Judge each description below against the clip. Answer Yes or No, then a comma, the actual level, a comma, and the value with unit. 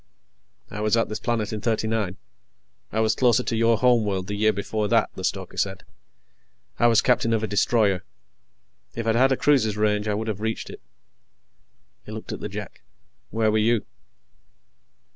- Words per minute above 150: Yes, average, 180 wpm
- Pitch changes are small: Yes, narrow, 1.7 semitones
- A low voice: Yes, low, 110 Hz